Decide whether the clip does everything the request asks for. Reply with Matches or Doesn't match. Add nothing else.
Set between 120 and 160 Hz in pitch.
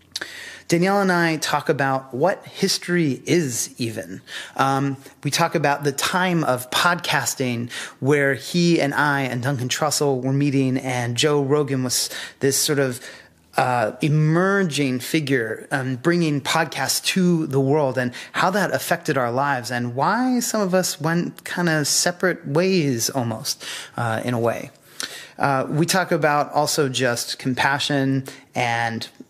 Matches